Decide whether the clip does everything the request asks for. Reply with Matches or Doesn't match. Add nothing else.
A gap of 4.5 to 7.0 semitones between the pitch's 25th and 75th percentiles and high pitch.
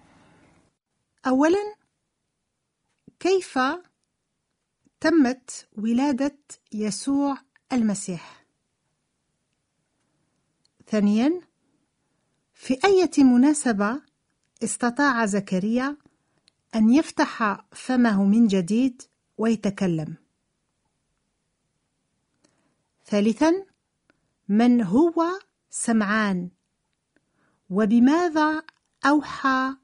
Matches